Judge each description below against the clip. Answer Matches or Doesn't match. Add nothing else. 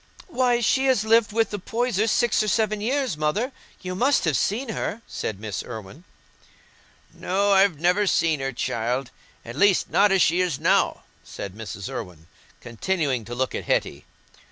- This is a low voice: Doesn't match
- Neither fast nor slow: Matches